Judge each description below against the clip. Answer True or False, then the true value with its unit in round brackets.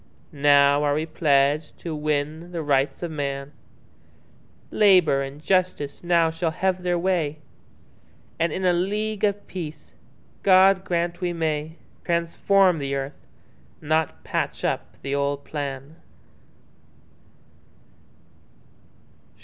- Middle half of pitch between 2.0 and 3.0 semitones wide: False (3.7 semitones)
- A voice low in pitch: False (160 Hz)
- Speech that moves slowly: True (100 wpm)